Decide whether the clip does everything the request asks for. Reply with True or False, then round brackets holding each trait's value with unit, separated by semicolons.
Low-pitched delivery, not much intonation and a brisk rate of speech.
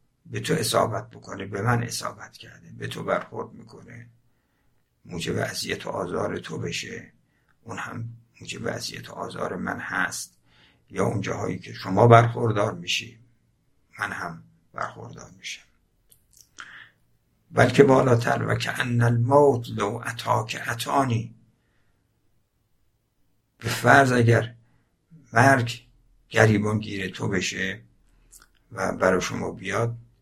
False (115 Hz; 2.3 semitones; 115 wpm)